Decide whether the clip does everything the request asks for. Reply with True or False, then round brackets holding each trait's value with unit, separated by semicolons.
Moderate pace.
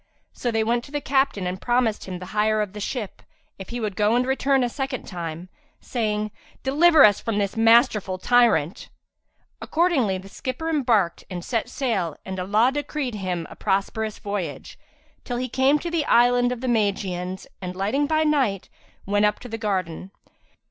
True (180 wpm)